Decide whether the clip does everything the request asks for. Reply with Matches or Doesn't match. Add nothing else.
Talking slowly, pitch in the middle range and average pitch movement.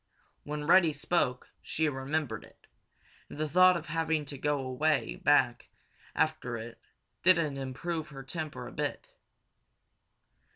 Matches